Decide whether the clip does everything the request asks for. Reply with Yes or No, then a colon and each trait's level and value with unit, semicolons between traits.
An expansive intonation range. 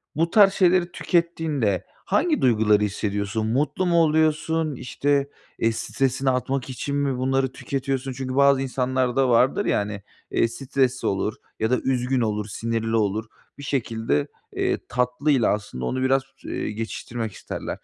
No: average, 3.9 semitones